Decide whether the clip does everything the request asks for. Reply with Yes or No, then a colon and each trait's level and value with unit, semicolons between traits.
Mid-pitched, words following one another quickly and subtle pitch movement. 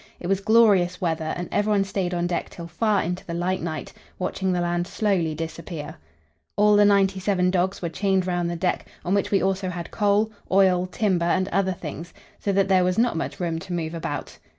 Yes: medium, 180 Hz; fast, 210 wpm; narrow, 2.3 semitones